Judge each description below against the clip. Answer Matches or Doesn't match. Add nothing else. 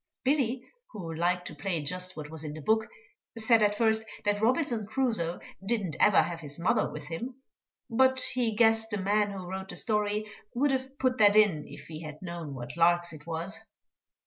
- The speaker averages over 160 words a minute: Matches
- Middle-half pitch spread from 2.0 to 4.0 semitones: Doesn't match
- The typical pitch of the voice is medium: Doesn't match